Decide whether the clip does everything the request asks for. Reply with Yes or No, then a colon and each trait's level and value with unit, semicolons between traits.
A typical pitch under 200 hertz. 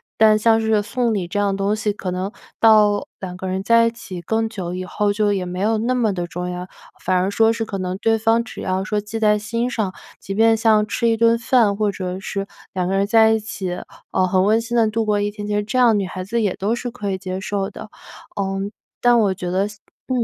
No: high, 210 Hz